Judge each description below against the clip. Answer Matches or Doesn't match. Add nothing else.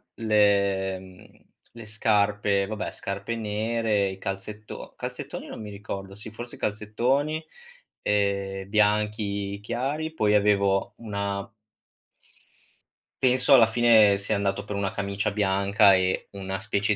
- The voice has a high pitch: Doesn't match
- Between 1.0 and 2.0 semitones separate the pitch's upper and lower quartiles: Matches